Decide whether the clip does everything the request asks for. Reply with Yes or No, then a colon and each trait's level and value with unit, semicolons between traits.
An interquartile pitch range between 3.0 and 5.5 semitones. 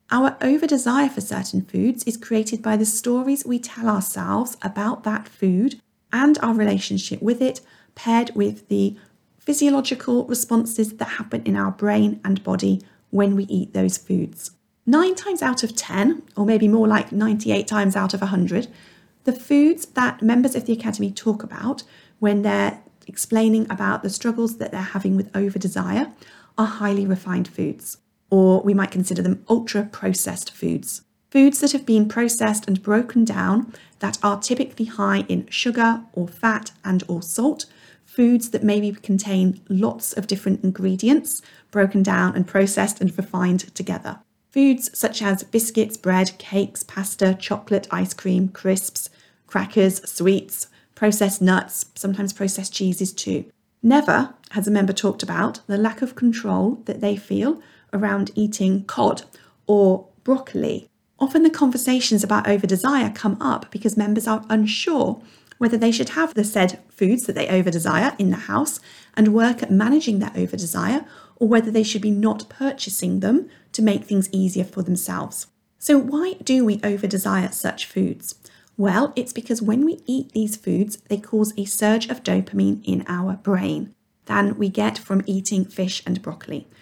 Yes: average, 3.3 semitones